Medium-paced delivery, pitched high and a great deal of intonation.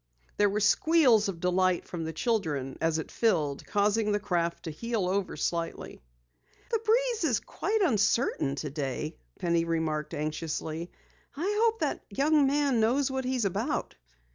Yes: average, 155 wpm; high, 200 Hz; wide, 8.3 semitones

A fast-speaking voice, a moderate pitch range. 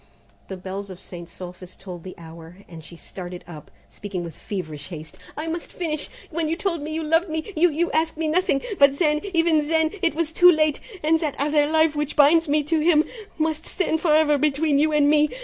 No: fast, 220 wpm; wide, 8.9 semitones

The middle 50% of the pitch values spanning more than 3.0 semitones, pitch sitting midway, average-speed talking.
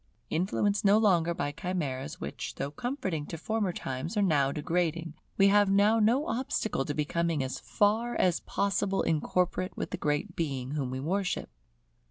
Yes: wide, 5.5 semitones; medium, 175 Hz; average, 165 wpm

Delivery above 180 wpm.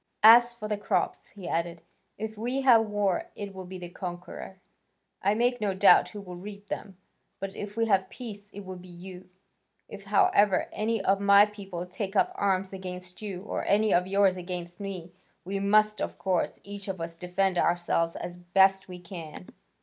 Yes: average, 190 wpm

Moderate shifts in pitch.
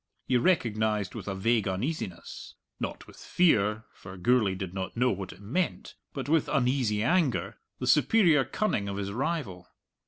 No: wide, 6.0 semitones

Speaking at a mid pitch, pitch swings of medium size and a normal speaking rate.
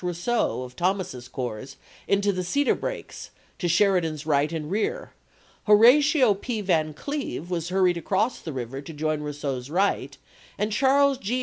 No: medium, 180 Hz; wide, 6.3 semitones; average, 150 wpm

